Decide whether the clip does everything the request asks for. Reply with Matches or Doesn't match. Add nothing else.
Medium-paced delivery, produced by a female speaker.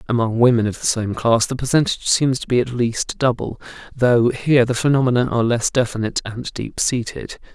Doesn't match